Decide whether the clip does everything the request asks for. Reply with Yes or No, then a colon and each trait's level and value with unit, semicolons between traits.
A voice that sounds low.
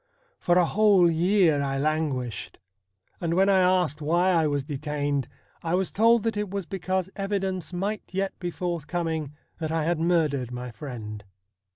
No: medium, 170 Hz